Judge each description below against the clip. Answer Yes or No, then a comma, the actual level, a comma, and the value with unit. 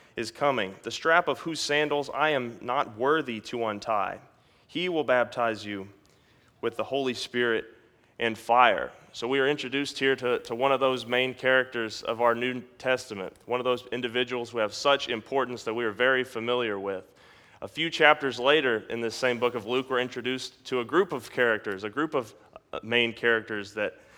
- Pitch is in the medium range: No, low, 125 Hz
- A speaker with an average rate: Yes, average, 190 wpm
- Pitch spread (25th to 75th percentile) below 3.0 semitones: Yes, narrow, 2.4 semitones